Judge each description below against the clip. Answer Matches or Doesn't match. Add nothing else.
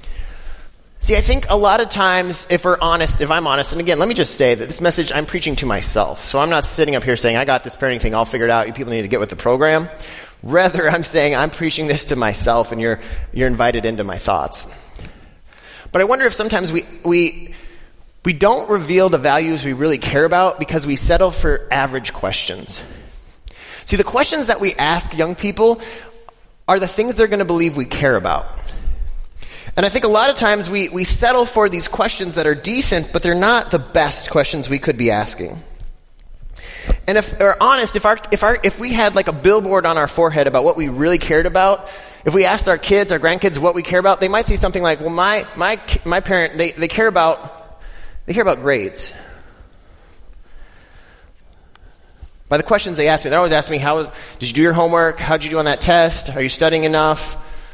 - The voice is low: Doesn't match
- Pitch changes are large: Matches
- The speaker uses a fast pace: Matches